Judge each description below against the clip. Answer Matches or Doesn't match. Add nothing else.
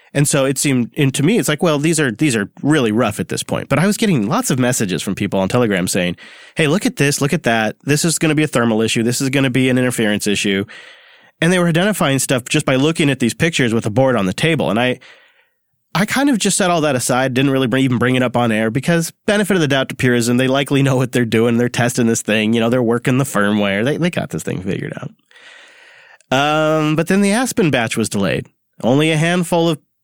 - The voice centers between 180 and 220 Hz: Doesn't match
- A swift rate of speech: Matches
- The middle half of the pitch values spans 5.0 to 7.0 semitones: Matches